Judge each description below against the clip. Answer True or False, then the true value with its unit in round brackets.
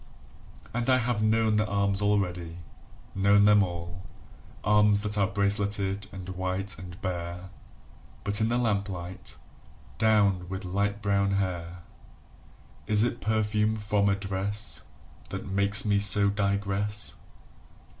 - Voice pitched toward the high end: False (100 Hz)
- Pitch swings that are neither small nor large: False (1.7 semitones)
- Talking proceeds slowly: True (125 wpm)